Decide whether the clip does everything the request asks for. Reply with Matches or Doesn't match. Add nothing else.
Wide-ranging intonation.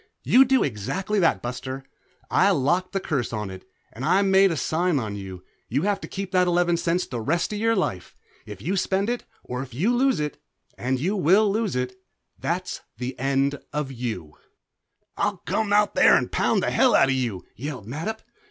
Matches